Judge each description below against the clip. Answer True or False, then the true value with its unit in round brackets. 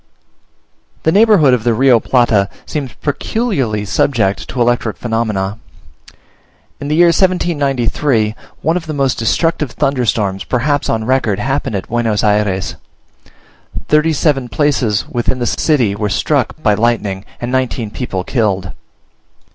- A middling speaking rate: False (130 wpm)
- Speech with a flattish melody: False (5.2 semitones)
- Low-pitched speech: True (120 Hz)